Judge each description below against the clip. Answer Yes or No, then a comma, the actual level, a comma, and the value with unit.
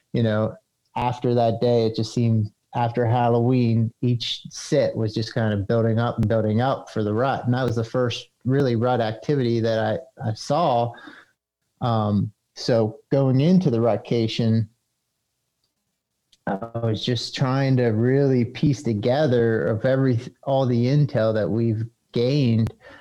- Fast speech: No, average, 150 wpm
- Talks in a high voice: No, low, 120 Hz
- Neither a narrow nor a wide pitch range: No, narrow, 2.2 semitones